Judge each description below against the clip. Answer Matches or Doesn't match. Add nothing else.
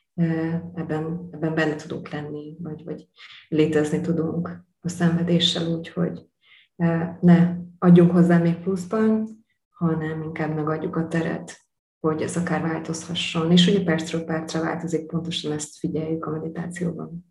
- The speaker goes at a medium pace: Matches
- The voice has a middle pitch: Matches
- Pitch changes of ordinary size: Doesn't match